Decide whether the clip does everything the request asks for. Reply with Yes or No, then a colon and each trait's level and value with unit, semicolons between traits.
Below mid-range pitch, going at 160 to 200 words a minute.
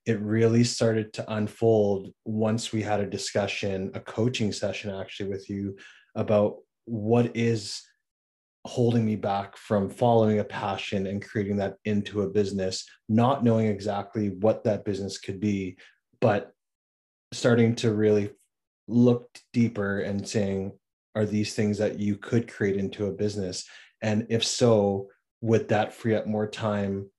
No: low, 105 Hz; average, 150 wpm